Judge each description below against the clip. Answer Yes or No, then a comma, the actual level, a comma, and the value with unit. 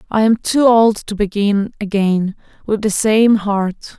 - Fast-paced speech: No, average, 165 wpm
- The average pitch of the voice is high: Yes, high, 210 Hz